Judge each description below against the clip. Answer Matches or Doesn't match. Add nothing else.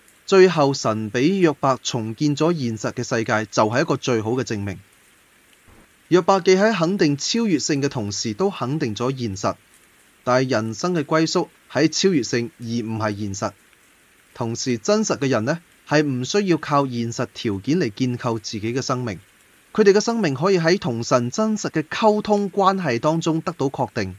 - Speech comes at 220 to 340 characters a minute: Matches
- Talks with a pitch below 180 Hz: Matches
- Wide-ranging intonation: Matches